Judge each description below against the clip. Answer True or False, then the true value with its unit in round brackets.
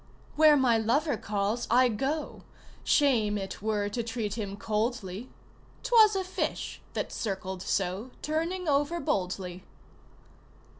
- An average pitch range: False (6.2 semitones)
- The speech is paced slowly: True (120 wpm)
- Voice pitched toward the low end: False (230 Hz)